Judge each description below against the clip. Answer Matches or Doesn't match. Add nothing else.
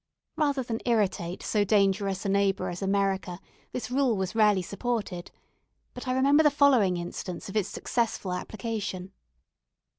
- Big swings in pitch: Doesn't match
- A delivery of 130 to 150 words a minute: Matches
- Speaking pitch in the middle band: Doesn't match